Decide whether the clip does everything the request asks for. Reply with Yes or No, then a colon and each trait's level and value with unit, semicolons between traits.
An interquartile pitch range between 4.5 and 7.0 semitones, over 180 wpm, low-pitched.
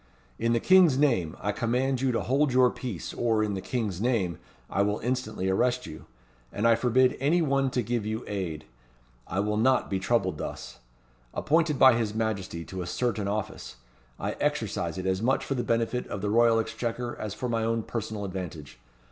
No: average, 3.9 semitones; average, 195 wpm; low, 115 Hz